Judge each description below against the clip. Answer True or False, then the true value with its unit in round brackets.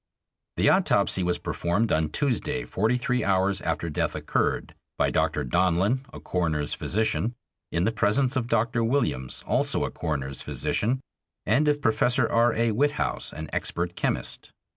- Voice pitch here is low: True (110 Hz)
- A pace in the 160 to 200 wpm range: False (150 wpm)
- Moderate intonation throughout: False (6.3 semitones)